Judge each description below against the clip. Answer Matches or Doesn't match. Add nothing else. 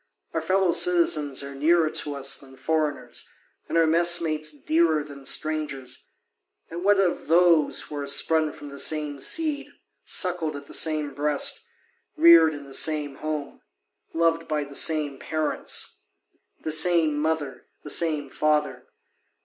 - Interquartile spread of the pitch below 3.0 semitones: Matches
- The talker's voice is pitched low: Doesn't match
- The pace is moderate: Matches